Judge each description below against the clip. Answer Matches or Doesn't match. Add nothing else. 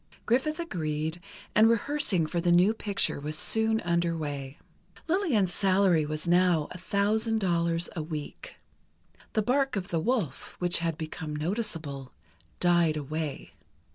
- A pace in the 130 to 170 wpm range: Matches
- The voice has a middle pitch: Matches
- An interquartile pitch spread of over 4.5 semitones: Matches